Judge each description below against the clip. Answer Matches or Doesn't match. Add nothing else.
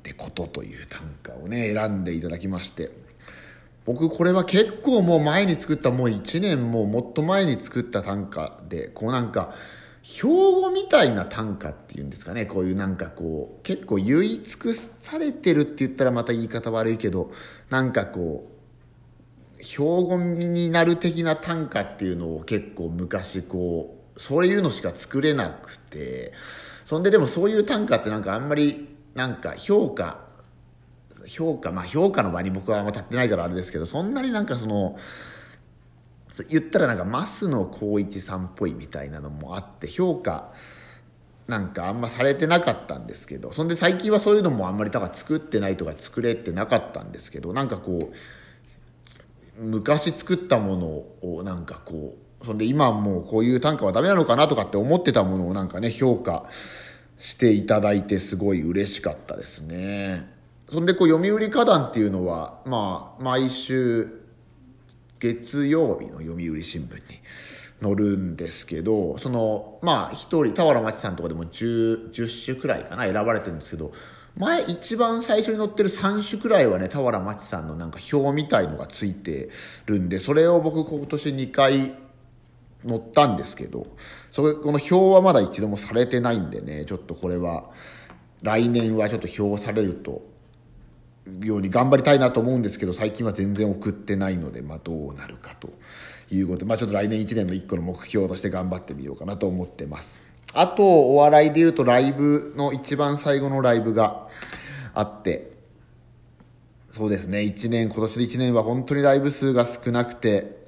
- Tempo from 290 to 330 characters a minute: Doesn't match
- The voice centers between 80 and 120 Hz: Matches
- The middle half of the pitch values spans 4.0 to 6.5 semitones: Doesn't match